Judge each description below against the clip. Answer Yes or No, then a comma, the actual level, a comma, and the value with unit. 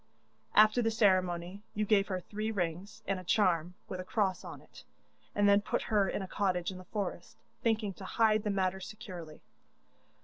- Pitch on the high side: Yes, high, 195 Hz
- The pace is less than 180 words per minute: No, average, 190 wpm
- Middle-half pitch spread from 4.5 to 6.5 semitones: No, narrow, 2.5 semitones